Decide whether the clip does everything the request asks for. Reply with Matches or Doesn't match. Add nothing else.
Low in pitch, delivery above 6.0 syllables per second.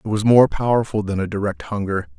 Doesn't match